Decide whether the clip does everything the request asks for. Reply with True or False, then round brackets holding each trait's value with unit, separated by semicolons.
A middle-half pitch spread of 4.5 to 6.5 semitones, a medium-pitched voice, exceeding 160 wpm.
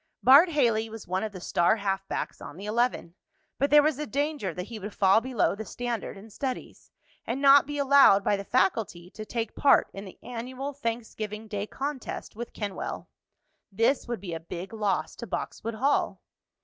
False (4.9 semitones; 225 Hz; 190 wpm)